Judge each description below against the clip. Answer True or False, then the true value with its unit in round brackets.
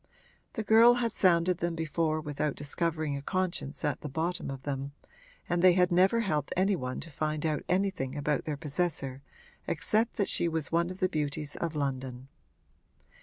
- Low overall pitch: False (160 Hz)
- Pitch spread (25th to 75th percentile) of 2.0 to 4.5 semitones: True (4.0 semitones)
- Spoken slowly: False (175 wpm)